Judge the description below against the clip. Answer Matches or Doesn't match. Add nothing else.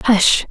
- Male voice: Doesn't match